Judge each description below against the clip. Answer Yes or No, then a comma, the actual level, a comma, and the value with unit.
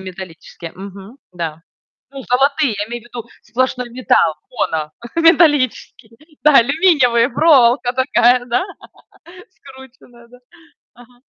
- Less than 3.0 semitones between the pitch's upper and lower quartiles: No, average, 3.7 semitones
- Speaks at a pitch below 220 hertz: No, high, 245 Hz